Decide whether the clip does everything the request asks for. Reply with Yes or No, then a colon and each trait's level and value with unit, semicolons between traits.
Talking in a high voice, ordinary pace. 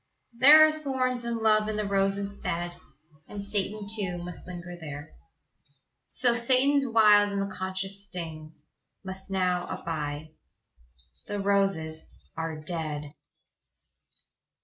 No: high, 195 Hz; slow, 120 wpm